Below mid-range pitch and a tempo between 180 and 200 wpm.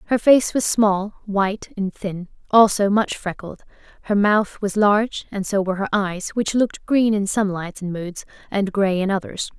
No: high, 200 Hz; average, 195 wpm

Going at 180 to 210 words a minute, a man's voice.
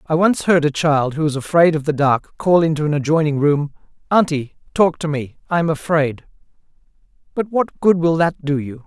Yes: fast, 205 wpm; male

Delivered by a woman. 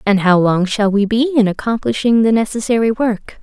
Yes: female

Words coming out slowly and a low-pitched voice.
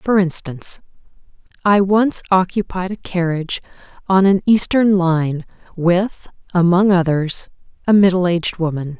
No: slow, 120 wpm; medium, 180 Hz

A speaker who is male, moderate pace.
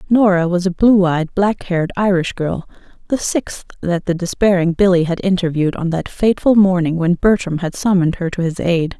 No: female; average, 195 wpm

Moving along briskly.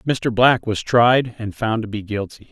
Yes: fast, 215 wpm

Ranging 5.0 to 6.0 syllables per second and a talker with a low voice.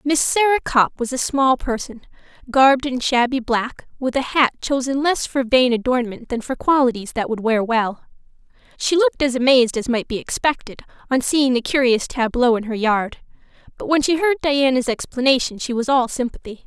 No: 5.2 syllables/s; very high, 255 Hz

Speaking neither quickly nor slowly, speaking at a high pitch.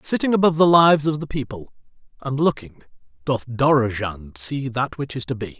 No: average, 180 wpm; low, 135 Hz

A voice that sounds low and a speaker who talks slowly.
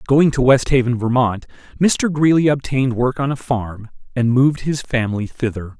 No: low, 130 Hz; average, 165 wpm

